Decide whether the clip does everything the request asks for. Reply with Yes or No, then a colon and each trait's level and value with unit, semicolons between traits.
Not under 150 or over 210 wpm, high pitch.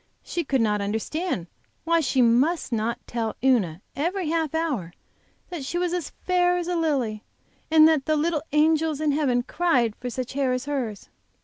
Yes: average, 180 wpm; very high, 290 Hz